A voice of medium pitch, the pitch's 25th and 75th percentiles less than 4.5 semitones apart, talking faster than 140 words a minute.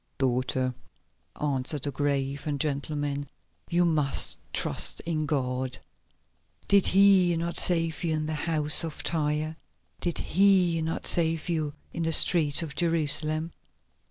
No: medium, 155 Hz; narrow, 2.5 semitones; slow, 135 wpm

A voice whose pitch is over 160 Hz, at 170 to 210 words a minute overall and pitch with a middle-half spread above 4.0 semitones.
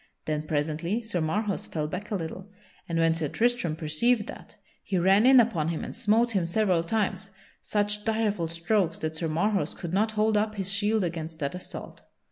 Yes: high, 190 Hz; average, 190 wpm; average, 4.6 semitones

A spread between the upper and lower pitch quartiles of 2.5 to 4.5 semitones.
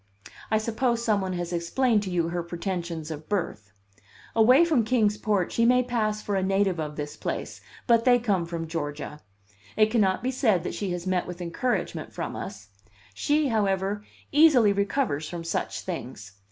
No: average, 5.2 semitones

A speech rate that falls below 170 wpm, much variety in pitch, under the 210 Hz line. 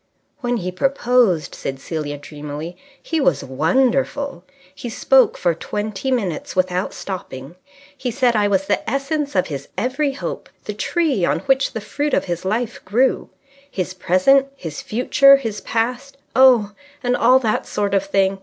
No: average, 160 wpm; wide, 6.5 semitones; high, 215 Hz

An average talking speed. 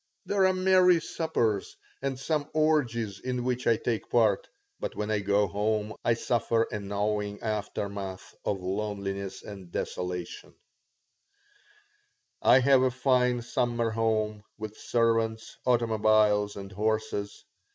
No: slow, 125 wpm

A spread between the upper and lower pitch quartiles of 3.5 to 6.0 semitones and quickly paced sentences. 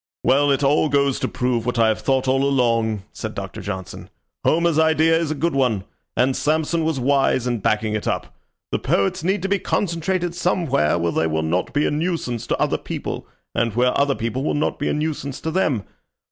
Yes: wide, 5.4 semitones; fast, 210 wpm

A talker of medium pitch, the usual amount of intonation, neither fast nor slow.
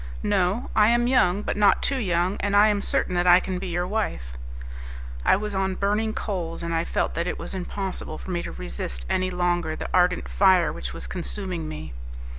No: medium, 180 Hz; average, 3.3 semitones; fast, 210 wpm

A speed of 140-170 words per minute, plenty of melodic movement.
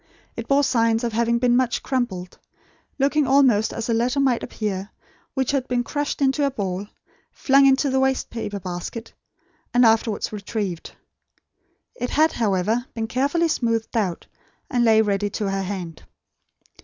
No: average, 155 wpm; average, 4.3 semitones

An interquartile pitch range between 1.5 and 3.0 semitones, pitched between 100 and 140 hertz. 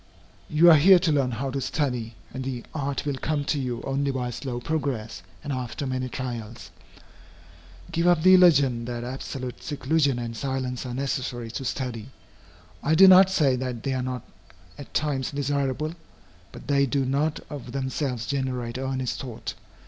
Yes: narrow, 2.5 semitones; low, 135 Hz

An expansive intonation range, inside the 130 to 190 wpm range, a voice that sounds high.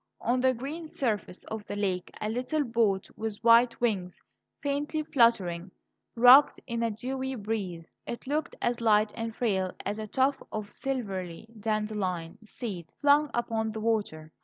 No: average, 3.6 semitones; average, 155 wpm; high, 225 Hz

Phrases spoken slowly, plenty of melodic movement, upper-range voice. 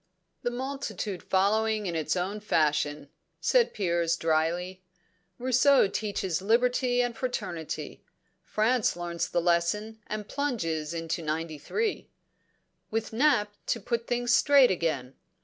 Yes: slow, 115 wpm; wide, 6.3 semitones; high, 205 Hz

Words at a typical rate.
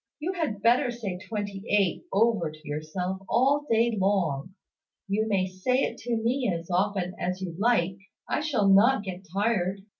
Yes: average, 170 wpm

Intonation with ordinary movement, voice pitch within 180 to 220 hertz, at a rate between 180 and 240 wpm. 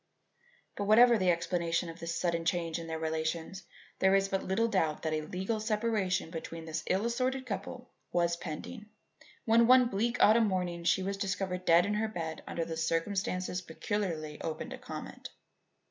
No: average, 4.2 semitones; medium, 185 Hz; average, 170 wpm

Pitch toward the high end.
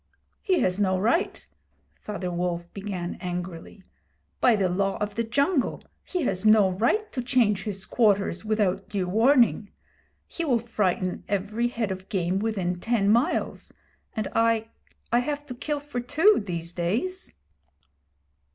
Yes: high, 210 Hz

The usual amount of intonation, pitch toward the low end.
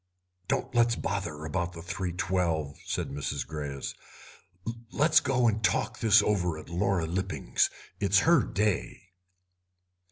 Yes: average, 4.2 semitones; very low, 95 Hz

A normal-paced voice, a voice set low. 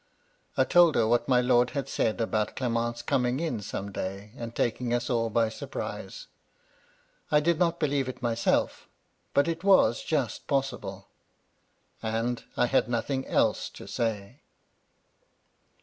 Yes: average, 150 wpm; low, 120 Hz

